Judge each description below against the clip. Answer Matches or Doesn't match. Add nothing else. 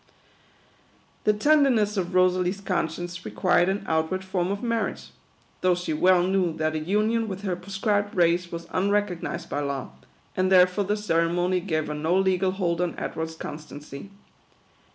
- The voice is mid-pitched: Matches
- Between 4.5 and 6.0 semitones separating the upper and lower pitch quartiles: Doesn't match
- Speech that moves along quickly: Doesn't match